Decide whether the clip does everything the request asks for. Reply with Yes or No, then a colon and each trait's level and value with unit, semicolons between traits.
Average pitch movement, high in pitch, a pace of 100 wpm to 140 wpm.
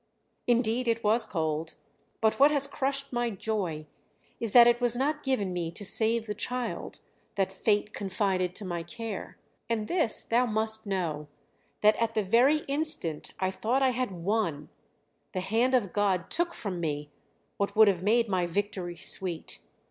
No: average, 4.5 semitones; high, 215 Hz; average, 170 wpm